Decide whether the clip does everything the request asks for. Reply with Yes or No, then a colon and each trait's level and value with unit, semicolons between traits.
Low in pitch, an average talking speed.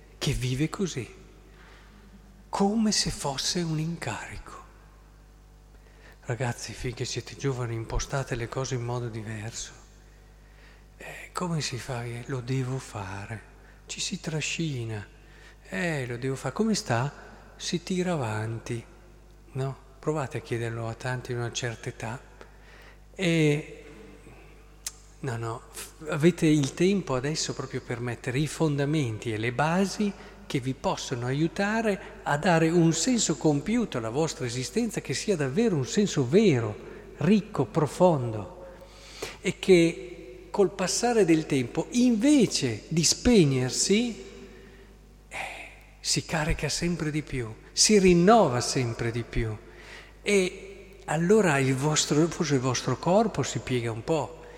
No: medium, 150 Hz; average, 130 wpm